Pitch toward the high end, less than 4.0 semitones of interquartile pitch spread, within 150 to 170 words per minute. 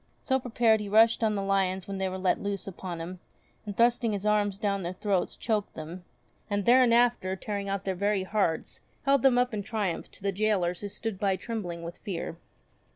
No: high, 200 Hz; average, 2.8 semitones; fast, 205 wpm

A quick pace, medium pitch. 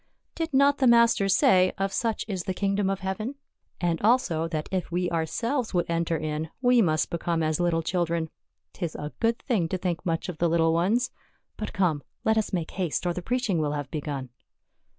Yes: fast, 210 wpm; medium, 180 Hz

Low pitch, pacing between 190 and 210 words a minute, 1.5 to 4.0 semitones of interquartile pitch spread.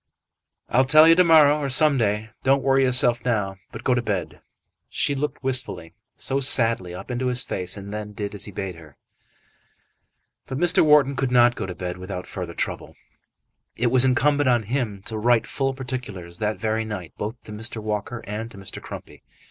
No: low, 120 Hz; average, 195 wpm; average, 4.4 semitones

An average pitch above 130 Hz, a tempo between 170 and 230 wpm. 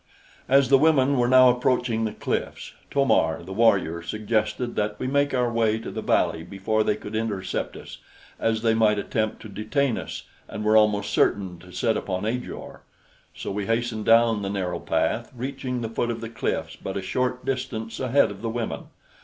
No: low, 115 Hz; average, 195 wpm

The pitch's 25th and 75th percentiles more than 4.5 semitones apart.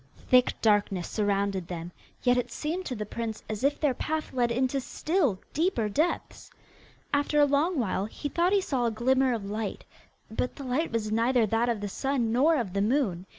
Yes: average, 5.1 semitones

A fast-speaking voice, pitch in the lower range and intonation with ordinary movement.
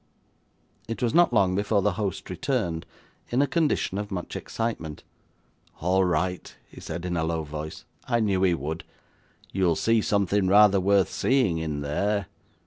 No: average, 160 wpm; very low, 95 Hz; average, 4.0 semitones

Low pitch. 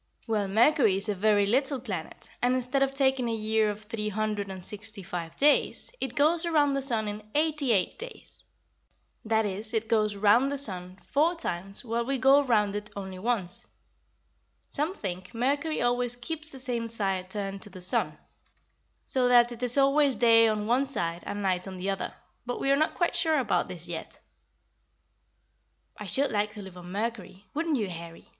No: high, 225 Hz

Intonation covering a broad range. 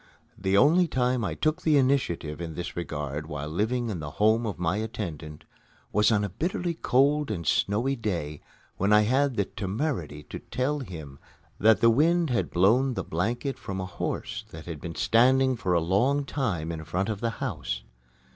Yes: wide, 7.4 semitones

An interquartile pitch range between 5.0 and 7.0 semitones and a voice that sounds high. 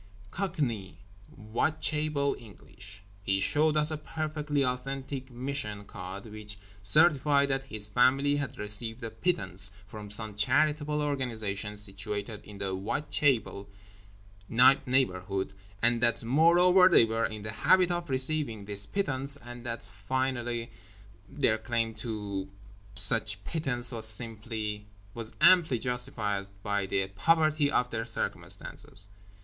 No: average, 5.3 semitones; low, 115 Hz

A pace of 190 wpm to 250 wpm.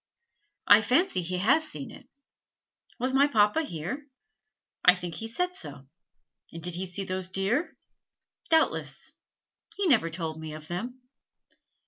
No: average, 140 wpm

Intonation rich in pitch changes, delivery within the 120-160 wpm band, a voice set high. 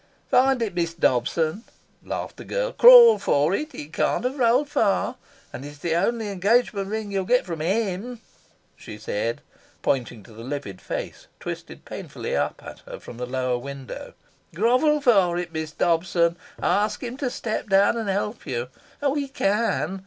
No: wide, 7.5 semitones; average, 170 wpm; high, 195 Hz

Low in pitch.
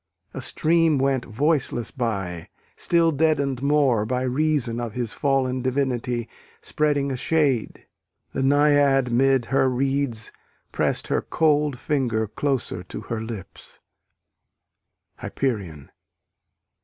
Yes: low, 130 Hz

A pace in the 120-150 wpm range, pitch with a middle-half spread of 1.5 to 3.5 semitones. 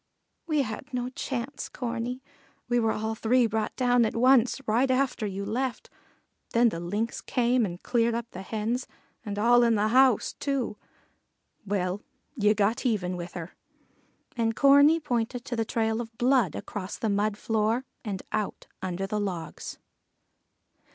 No: average, 160 wpm; average, 3.1 semitones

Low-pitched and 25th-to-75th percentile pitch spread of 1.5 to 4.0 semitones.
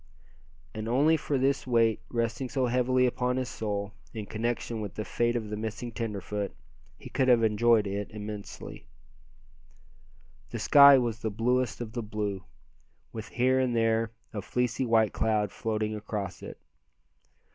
Yes: low, 115 Hz; average, 2.7 semitones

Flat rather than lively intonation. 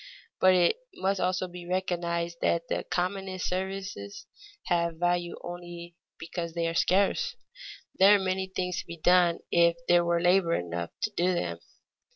Yes: narrow, 1.6 semitones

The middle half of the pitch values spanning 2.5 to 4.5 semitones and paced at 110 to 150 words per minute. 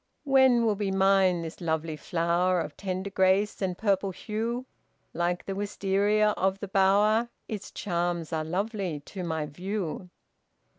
Yes: average, 2.9 semitones; average, 145 wpm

